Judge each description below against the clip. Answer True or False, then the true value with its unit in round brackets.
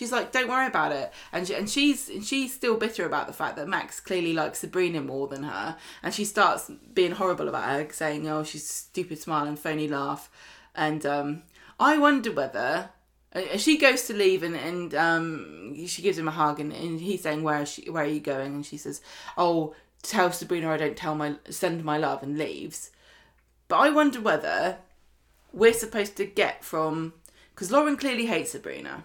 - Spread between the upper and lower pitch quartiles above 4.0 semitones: True (5.2 semitones)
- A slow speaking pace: False (200 wpm)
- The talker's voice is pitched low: False (170 Hz)